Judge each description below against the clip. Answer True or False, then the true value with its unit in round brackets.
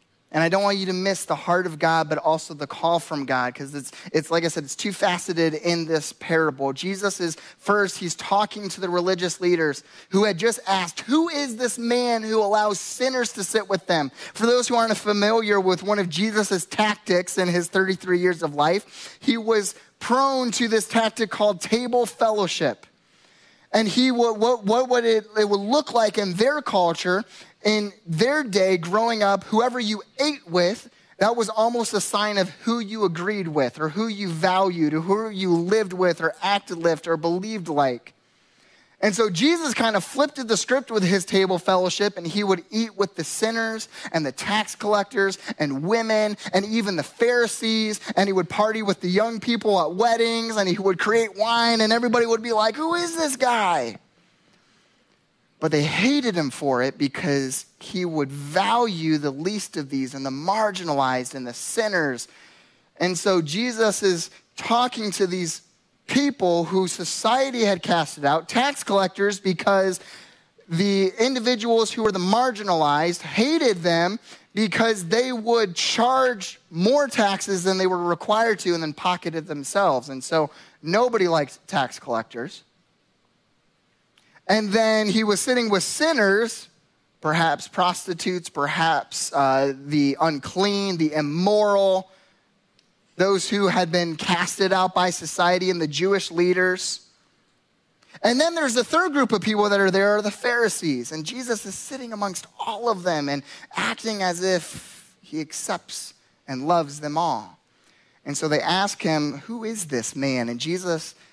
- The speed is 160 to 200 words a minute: True (170 wpm)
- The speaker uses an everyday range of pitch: True (4.6 semitones)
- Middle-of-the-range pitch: False (195 Hz)